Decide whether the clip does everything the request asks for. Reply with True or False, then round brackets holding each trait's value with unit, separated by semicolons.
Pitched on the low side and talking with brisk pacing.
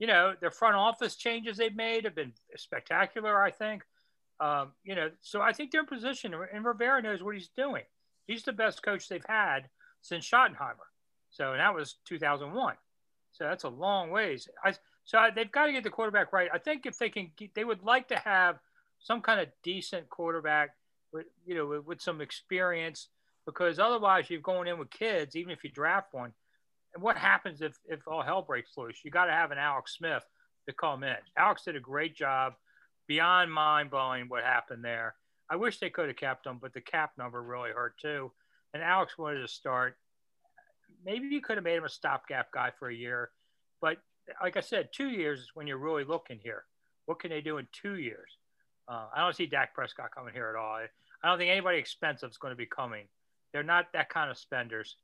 False (175 Hz; 215 wpm)